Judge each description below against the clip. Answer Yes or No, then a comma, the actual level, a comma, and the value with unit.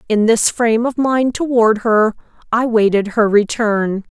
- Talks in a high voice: Yes, high, 225 Hz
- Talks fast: No, average, 160 wpm